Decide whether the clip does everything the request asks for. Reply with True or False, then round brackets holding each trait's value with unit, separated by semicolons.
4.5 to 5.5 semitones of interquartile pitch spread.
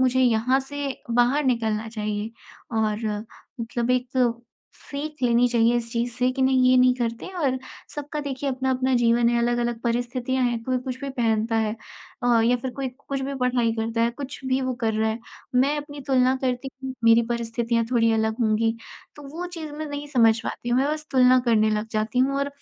False (2.4 semitones)